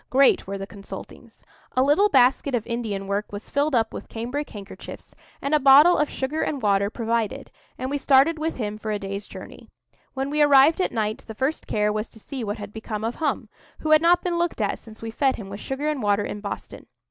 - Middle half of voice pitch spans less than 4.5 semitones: No, wide, 5.4 semitones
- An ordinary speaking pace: No, fast, 230 wpm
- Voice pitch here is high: Yes, high, 245 Hz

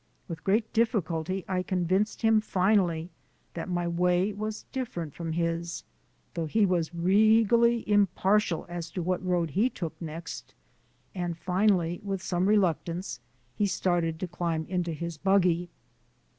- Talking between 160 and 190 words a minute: No, average, 140 wpm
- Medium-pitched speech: Yes, medium, 180 Hz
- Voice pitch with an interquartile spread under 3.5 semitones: Yes, average, 3.1 semitones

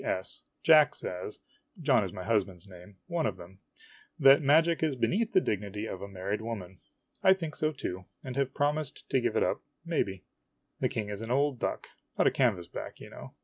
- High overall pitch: No, low, 115 Hz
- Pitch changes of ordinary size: No, wide, 7.5 semitones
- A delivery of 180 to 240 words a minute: Yes, average, 200 wpm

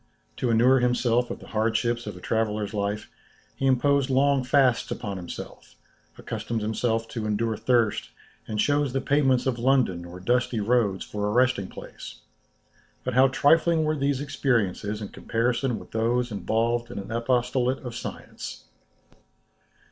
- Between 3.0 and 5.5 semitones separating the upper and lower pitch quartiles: Yes, average, 3.3 semitones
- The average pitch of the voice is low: Yes, low, 120 Hz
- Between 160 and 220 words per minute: No, average, 150 wpm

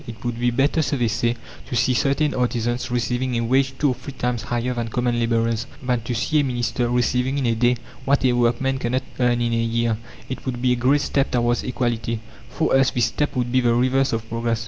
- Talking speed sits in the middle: No, fast, 235 wpm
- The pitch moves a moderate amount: No, narrow, 1.7 semitones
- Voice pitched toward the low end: Yes, low, 120 Hz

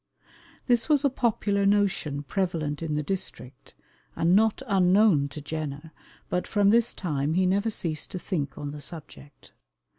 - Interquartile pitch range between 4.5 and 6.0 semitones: Yes, wide, 5.5 semitones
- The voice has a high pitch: No, medium, 180 Hz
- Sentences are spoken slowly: No, average, 155 wpm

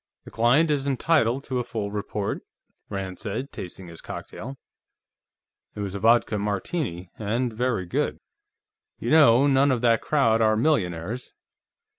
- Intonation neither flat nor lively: Yes, average, 4.7 semitones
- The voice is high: No, low, 115 Hz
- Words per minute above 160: No, average, 145 wpm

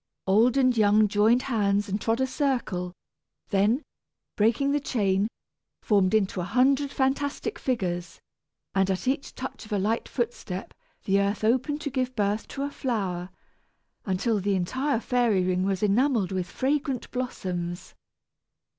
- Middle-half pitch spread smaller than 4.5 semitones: No, average, 5.1 semitones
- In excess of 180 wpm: No, average, 145 wpm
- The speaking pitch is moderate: No, high, 215 Hz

